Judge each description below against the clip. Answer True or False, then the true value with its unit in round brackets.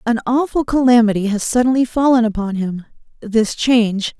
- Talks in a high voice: True (230 Hz)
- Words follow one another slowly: True (130 wpm)